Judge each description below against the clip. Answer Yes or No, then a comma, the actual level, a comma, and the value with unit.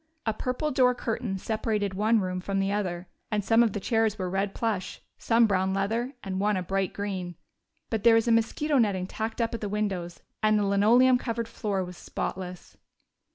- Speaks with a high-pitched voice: Yes, high, 210 Hz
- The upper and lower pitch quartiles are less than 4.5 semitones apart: Yes, average, 3.0 semitones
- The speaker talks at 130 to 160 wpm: No, average, 200 wpm